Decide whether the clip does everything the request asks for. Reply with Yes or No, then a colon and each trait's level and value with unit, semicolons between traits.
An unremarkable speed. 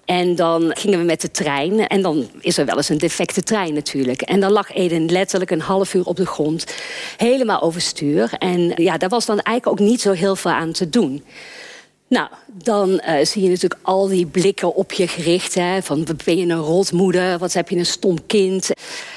No: fast, 215 wpm